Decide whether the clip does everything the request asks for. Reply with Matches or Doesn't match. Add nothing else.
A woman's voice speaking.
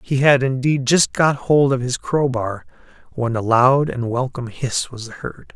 Doesn't match